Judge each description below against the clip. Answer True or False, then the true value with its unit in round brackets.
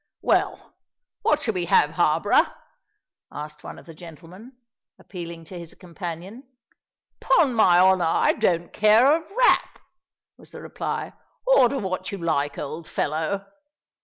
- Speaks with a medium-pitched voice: True (180 Hz)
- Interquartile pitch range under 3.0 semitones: False (4.8 semitones)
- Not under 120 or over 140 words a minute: True (135 wpm)